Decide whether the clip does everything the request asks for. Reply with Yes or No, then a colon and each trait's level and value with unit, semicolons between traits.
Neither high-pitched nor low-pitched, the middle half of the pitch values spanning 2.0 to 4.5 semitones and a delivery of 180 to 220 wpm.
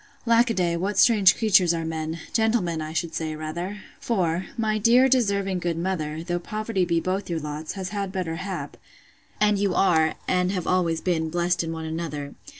Yes: medium, 180 Hz; average, 3.6 semitones; average, 190 wpm